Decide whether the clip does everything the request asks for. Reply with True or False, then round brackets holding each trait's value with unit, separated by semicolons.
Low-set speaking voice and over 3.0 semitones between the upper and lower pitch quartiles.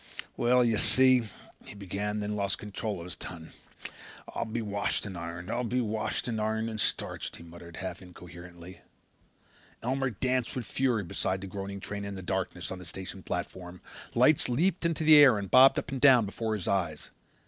True (105 Hz; 4.8 semitones)